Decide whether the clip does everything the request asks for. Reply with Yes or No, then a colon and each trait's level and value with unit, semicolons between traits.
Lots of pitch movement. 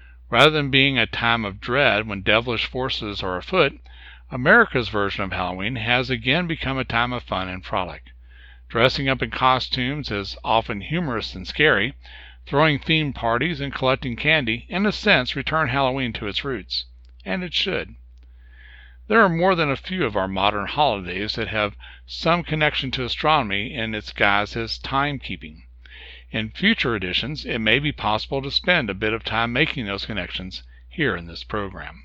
Yes: wide, 6.5 semitones